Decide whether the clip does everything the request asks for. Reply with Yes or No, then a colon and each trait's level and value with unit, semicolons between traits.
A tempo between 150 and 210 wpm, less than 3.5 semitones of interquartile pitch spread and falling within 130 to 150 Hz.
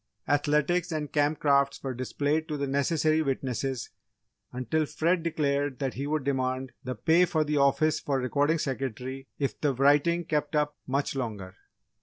Yes: average, 160 wpm; narrow, 2.5 semitones; medium, 140 Hz